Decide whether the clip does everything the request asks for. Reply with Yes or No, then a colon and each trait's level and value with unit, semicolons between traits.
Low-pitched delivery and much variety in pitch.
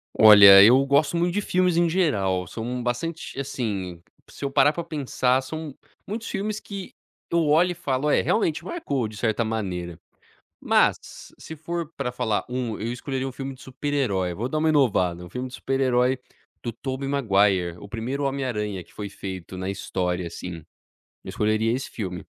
Yes: low, 125 Hz; wide, 6.2 semitones